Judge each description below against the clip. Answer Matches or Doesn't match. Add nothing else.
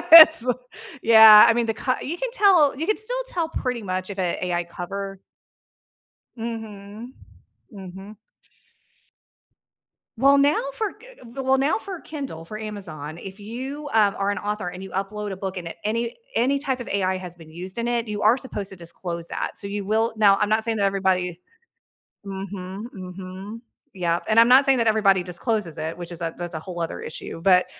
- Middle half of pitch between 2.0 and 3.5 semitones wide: Doesn't match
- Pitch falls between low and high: Doesn't match